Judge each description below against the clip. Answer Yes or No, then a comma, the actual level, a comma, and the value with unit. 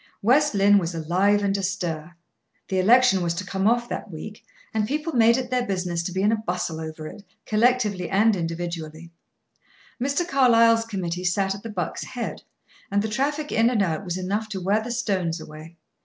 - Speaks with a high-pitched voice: Yes, high, 200 Hz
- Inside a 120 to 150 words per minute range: No, average, 190 wpm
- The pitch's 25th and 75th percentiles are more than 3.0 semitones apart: Yes, average, 4.6 semitones